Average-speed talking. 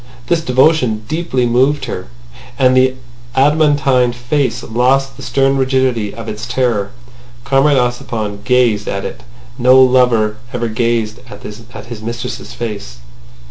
No: slow, 130 wpm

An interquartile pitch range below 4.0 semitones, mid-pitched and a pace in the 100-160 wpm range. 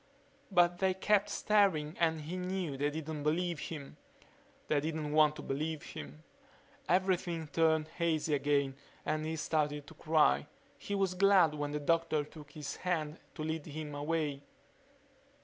Yes: narrow, 2.6 semitones; medium, 155 Hz; average, 150 wpm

